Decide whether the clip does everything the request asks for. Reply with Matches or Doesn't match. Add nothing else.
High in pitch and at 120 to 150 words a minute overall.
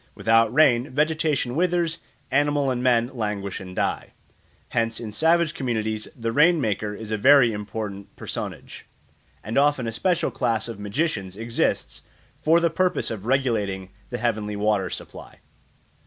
Doesn't match